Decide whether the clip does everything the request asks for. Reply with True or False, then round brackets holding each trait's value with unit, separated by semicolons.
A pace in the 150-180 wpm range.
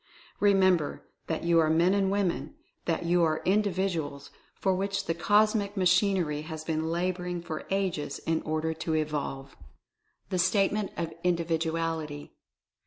False (140 wpm)